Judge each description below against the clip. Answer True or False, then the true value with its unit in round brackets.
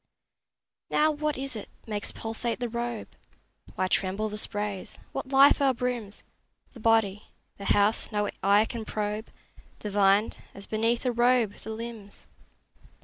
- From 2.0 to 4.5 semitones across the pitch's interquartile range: True (2.7 semitones)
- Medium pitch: False (220 Hz)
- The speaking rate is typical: True (145 wpm)